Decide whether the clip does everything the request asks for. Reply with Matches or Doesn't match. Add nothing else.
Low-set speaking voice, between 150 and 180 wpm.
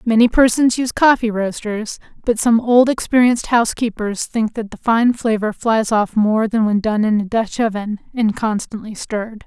Doesn't match